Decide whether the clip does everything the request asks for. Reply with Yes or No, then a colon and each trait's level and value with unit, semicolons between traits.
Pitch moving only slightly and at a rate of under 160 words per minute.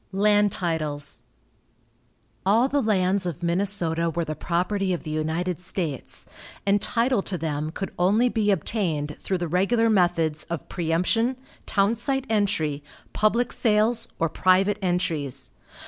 No: average, 4.3 semitones; slow, 135 wpm